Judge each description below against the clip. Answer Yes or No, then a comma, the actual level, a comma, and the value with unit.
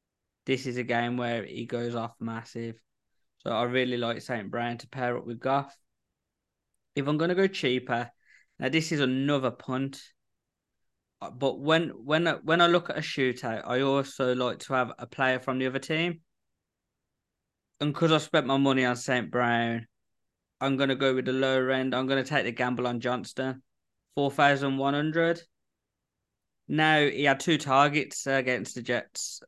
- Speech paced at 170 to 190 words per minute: Yes, average, 175 wpm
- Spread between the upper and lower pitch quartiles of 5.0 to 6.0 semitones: No, average, 2.8 semitones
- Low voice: Yes, low, 130 Hz